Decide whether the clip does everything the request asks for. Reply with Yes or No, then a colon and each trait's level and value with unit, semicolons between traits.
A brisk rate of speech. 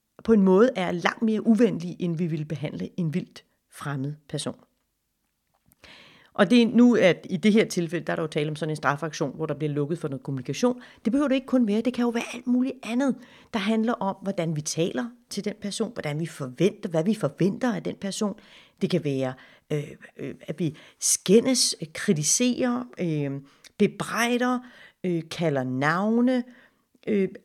No: average, 175 wpm